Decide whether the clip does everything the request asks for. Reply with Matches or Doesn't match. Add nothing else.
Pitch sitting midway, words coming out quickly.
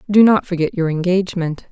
Doesn't match